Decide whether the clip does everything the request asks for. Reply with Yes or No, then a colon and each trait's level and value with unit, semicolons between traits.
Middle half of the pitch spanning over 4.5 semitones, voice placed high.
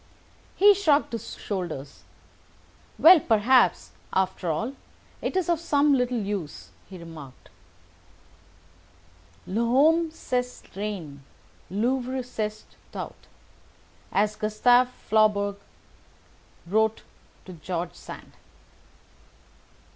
Yes: wide, 5.4 semitones; high, 215 Hz